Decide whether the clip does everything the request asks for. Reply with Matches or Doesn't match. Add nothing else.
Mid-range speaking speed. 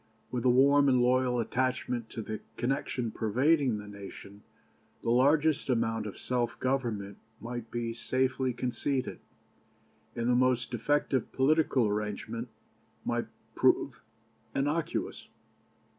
Doesn't match